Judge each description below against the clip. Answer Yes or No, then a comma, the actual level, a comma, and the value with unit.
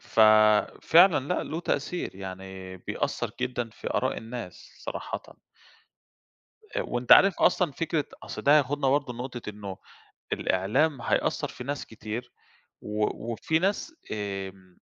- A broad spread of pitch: Yes, wide, 6.1 semitones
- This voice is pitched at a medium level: No, low, 120 Hz